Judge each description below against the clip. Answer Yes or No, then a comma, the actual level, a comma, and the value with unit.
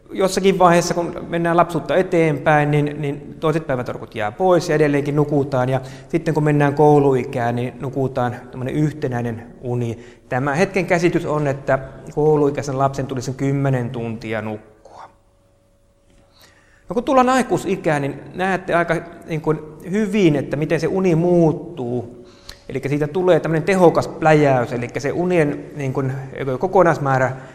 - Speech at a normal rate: Yes, average, 125 wpm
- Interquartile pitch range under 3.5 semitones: No, average, 4.8 semitones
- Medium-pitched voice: Yes, medium, 145 Hz